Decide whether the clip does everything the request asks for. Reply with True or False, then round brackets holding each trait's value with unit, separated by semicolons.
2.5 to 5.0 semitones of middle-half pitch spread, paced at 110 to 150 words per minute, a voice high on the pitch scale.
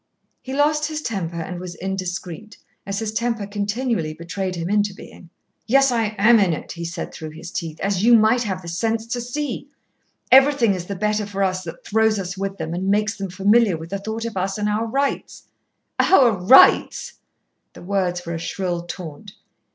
False (4.1 semitones; 195 wpm; 200 Hz)